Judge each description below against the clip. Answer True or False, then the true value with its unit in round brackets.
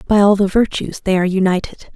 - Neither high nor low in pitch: False (195 Hz)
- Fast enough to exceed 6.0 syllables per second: True (6.3 syllables/s)